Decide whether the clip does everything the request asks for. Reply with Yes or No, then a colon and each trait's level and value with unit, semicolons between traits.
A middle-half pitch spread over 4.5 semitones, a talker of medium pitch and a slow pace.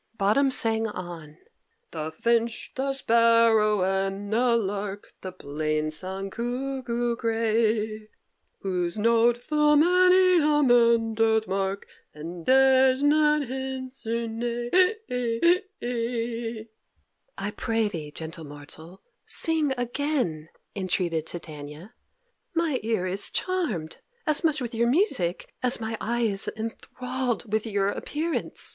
No: average, 5.0 semitones; high, 230 Hz; slow, 115 wpm